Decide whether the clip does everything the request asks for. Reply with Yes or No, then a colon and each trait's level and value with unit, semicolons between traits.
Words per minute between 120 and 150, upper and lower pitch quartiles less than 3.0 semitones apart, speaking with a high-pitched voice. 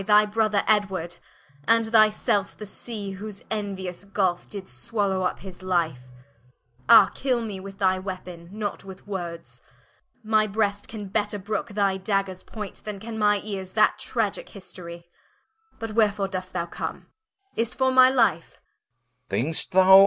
Yes: average, 145 wpm; narrow, 2.4 semitones; high, 200 Hz